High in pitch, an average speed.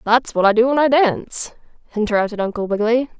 Yes: high, 230 Hz; average, 190 wpm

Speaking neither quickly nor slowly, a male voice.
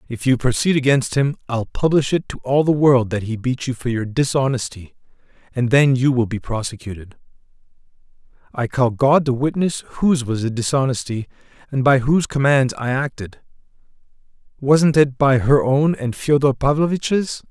Yes: average, 165 wpm; male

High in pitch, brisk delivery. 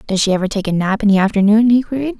Yes: high, 210 Hz; fast, 300 wpm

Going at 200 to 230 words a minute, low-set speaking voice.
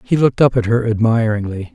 Yes: fast, 205 wpm; low, 115 Hz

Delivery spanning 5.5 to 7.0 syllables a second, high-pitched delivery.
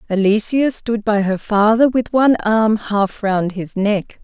No: 4.1 syllables/s; high, 215 Hz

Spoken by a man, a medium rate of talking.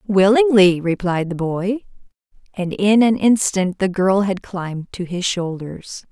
No: female; average, 145 wpm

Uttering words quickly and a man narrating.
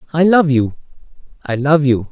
No: average, 140 wpm; male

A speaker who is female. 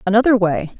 Yes: female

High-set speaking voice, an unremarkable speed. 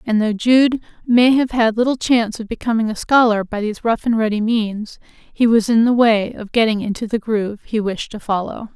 No: high, 225 Hz; fast, 220 wpm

